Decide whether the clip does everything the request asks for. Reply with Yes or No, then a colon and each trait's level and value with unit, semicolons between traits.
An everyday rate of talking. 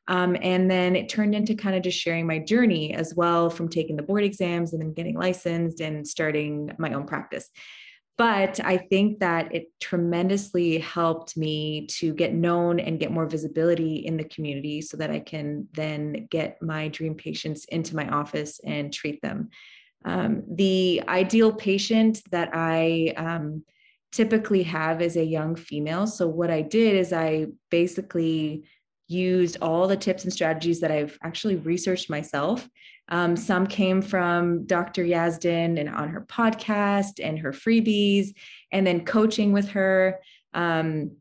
Yes: average, 160 wpm